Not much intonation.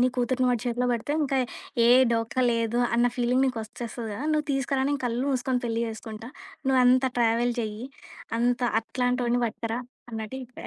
Yes: narrow, 1.9 semitones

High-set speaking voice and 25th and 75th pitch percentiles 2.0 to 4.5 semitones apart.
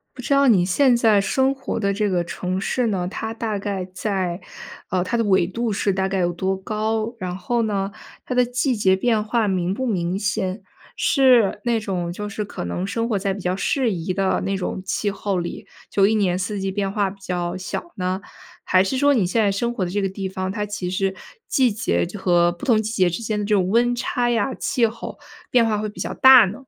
Yes: high, 200 Hz; average, 3.4 semitones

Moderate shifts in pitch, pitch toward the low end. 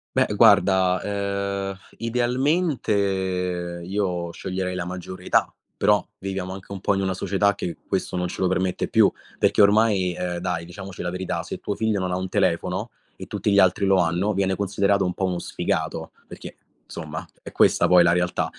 No: narrow, 1.9 semitones; very low, 95 Hz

